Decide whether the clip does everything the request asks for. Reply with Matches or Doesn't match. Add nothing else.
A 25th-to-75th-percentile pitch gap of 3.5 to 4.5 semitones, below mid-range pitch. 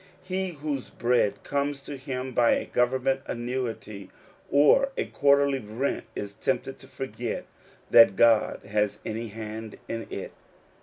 Matches